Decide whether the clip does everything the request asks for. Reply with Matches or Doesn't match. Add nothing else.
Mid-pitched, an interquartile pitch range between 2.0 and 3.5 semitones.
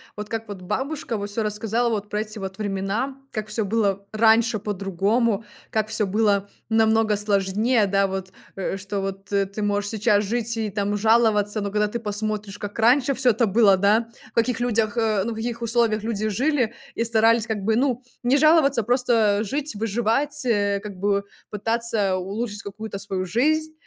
Doesn't match